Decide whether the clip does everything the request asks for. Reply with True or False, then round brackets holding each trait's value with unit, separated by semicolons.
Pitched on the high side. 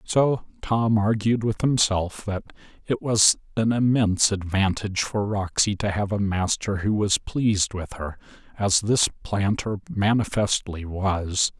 False (105 Hz)